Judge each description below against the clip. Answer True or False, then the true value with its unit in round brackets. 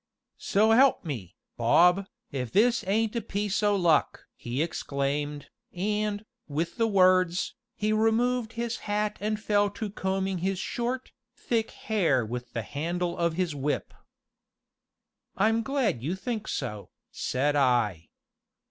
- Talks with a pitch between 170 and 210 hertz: True (190 Hz)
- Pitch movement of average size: False (6.8 semitones)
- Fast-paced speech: False (135 wpm)